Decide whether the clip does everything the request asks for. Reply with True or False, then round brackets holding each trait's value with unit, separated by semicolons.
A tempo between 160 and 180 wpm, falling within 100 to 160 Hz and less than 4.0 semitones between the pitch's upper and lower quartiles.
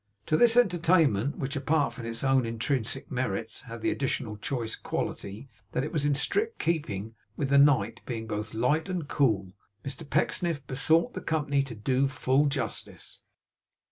False (165 wpm; 135 Hz; 4.4 semitones)